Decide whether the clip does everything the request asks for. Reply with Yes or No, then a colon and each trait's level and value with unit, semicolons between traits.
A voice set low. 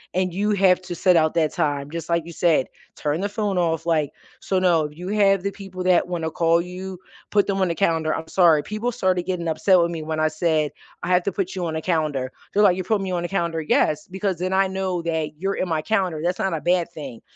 No: medium, 175 Hz